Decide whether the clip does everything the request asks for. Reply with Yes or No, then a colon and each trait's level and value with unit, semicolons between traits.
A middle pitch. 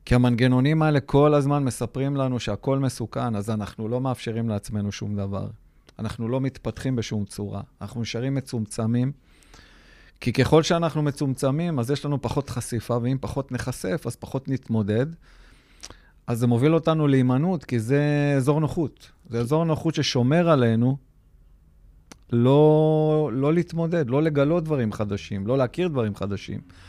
No: low, 125 Hz